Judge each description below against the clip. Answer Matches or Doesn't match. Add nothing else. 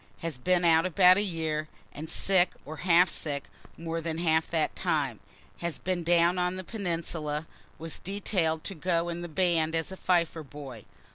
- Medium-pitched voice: Matches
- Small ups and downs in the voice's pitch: Matches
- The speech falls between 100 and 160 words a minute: Doesn't match